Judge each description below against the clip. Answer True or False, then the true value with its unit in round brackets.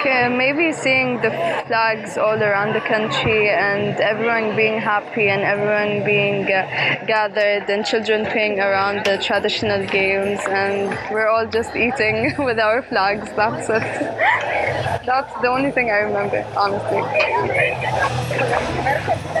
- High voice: True (210 Hz)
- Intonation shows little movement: True (2.1 semitones)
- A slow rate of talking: True (125 wpm)